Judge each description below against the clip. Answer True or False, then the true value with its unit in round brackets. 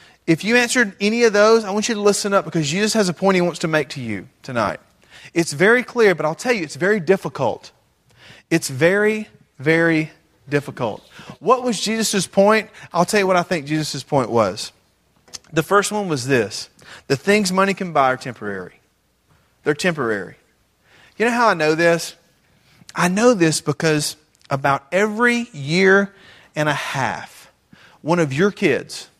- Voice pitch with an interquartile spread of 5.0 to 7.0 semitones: True (5.3 semitones)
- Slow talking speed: False (175 wpm)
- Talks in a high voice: False (175 Hz)